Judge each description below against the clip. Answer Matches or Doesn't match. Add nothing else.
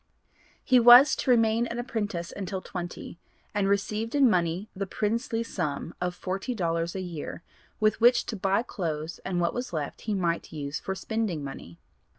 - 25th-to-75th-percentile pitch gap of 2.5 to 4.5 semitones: Doesn't match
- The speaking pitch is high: Matches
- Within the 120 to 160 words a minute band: Doesn't match